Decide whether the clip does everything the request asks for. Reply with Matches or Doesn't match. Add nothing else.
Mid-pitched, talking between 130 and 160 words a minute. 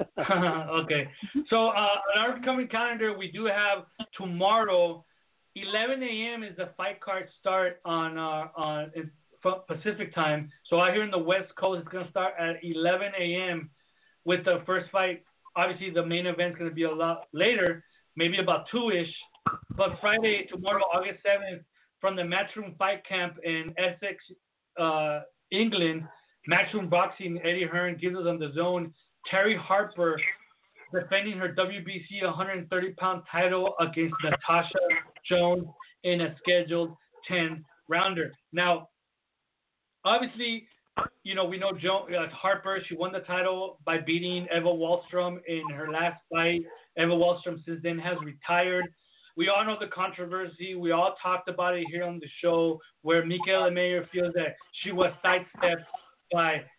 Matches